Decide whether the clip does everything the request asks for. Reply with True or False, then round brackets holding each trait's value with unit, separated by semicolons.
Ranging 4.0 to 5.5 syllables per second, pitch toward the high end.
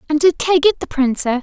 True (5.4 syllables/s; 305 Hz)